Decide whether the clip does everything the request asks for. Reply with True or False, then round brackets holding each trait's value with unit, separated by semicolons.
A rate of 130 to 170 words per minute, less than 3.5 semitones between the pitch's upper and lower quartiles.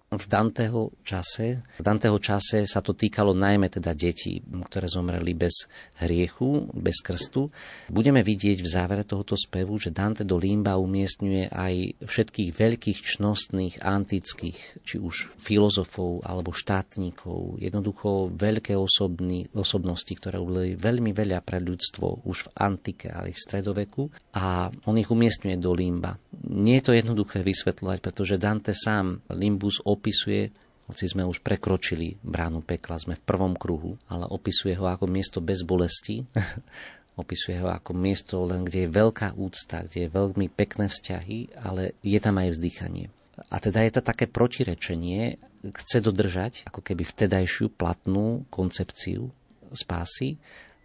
True (145 wpm; 2.7 semitones)